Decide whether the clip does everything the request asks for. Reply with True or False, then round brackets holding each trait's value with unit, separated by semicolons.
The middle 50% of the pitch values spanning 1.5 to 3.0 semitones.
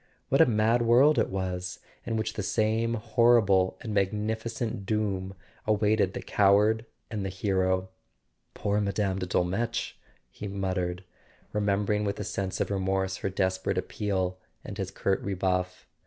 True (2.5 semitones)